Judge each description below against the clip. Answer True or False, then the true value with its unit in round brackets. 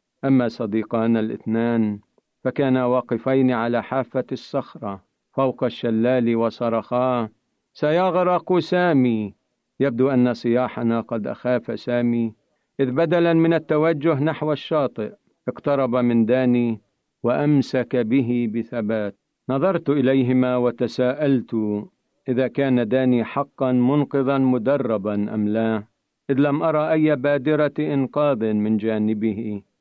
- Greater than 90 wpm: True (100 wpm)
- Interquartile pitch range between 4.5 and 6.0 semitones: False (3.4 semitones)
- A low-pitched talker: True (125 Hz)